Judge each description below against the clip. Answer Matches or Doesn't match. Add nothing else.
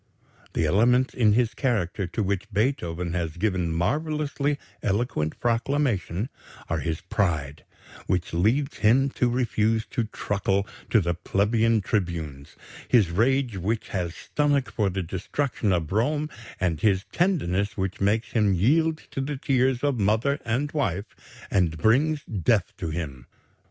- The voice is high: Doesn't match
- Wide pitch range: Matches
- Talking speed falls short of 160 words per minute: Matches